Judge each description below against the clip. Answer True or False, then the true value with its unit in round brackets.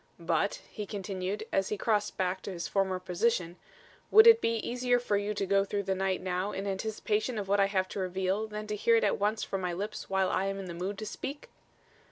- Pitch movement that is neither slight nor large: False (2.1 semitones)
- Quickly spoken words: True (240 wpm)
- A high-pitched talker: True (200 Hz)